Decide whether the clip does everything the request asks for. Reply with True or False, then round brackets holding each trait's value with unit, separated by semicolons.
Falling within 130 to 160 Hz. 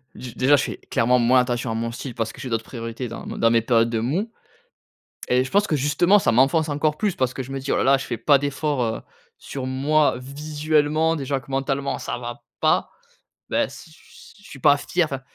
True (135 Hz)